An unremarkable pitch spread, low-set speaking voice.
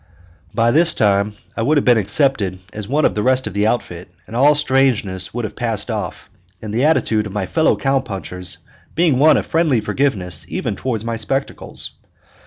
Yes: average, 4.8 semitones; low, 115 Hz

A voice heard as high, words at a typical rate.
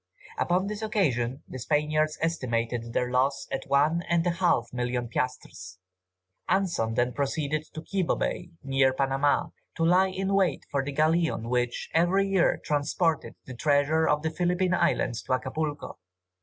No: medium, 150 Hz; average, 155 wpm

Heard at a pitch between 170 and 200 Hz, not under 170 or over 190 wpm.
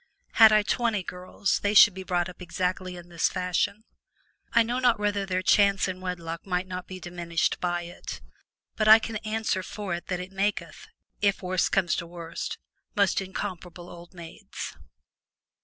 Yes: medium, 185 Hz; average, 175 wpm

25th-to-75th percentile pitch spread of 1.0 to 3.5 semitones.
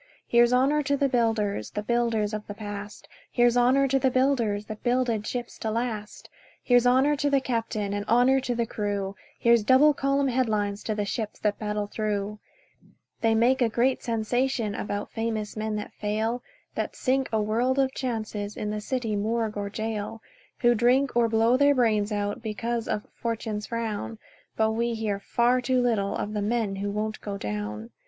Yes: average, 2.9 semitones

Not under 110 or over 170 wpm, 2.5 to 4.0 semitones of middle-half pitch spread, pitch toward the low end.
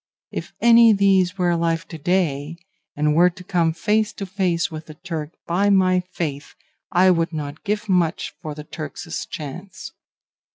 No: average, 165 wpm; average, 3.2 semitones; medium, 175 Hz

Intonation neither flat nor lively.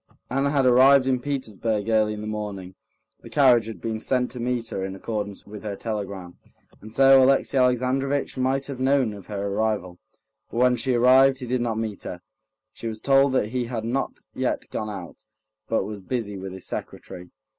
Yes: average, 3.8 semitones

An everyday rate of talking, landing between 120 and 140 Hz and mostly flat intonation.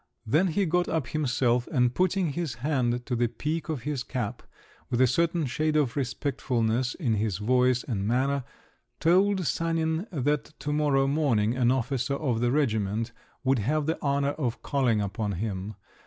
No: average, 170 wpm; low, 135 Hz; average, 4.3 semitones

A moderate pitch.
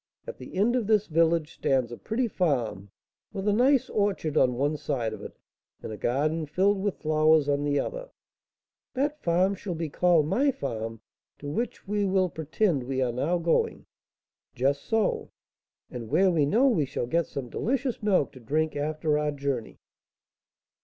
Yes: medium, 160 Hz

